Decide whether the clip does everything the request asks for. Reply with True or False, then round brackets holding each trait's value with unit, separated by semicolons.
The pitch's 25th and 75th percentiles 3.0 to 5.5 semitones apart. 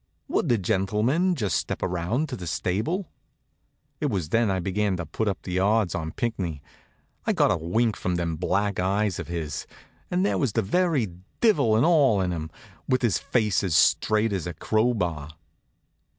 True (5.0 semitones)